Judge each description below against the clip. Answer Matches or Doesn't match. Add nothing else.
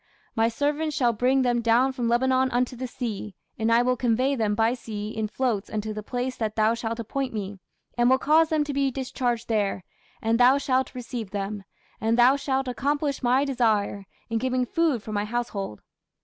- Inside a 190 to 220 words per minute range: Matches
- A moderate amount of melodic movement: Matches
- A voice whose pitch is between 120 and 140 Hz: Doesn't match